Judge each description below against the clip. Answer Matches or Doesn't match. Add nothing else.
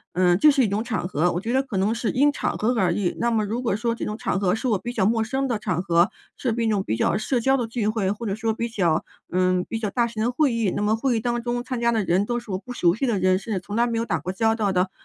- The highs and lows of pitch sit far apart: Doesn't match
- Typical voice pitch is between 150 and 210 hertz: Doesn't match